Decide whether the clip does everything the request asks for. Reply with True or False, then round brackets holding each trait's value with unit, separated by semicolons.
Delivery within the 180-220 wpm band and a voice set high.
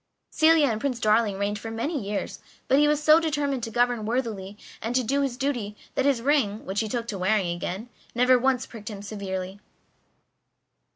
True (190 wpm; 230 Hz)